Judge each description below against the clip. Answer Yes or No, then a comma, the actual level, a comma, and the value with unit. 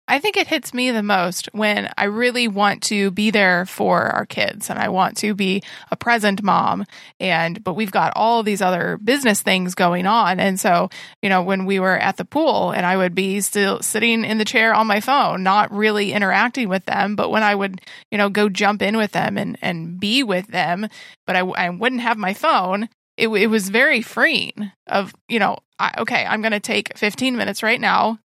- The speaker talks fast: Yes, fast, 220 wpm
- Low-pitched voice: No, high, 205 Hz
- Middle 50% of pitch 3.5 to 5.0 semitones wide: No, average, 2.8 semitones